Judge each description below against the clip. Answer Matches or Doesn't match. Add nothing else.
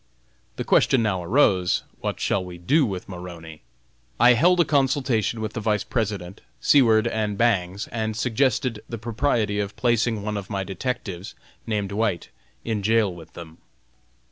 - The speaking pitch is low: Matches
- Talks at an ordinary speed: Matches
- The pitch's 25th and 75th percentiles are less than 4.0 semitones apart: Matches